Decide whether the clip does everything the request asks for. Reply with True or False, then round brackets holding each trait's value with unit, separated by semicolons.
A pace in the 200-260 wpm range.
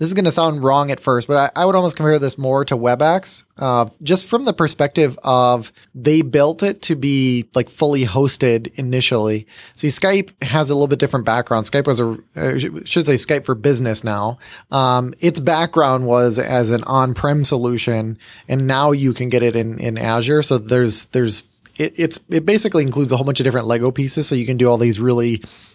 True (205 wpm)